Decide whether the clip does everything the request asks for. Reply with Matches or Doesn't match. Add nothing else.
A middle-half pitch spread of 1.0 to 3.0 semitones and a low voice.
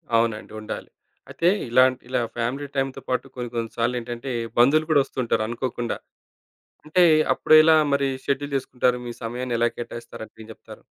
Matches